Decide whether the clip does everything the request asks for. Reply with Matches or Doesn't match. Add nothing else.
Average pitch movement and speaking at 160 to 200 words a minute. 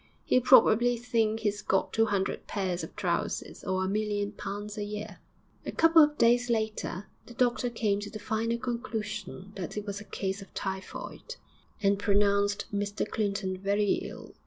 Doesn't match